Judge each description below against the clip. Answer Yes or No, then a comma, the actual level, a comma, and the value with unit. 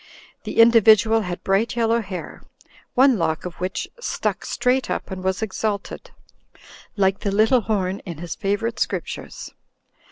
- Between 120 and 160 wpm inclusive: Yes, average, 140 wpm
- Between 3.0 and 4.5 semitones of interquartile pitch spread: Yes, average, 3.3 semitones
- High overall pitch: Yes, high, 205 Hz